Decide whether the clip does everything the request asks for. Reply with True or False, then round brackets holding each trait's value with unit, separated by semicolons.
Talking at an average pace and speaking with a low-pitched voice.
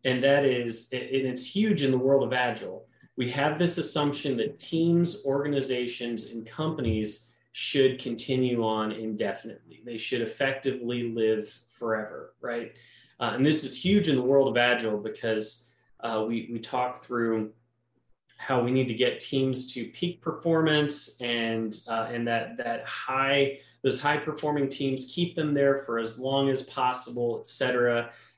True (160 wpm; 125 Hz)